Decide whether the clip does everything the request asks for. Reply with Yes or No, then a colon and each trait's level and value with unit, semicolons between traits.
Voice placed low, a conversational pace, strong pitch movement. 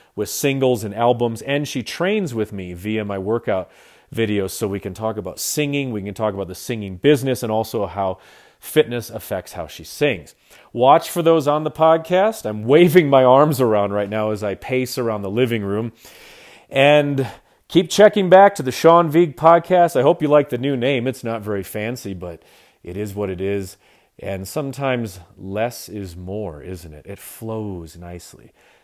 Yes: low, 115 Hz; average, 185 wpm; wide, 6.0 semitones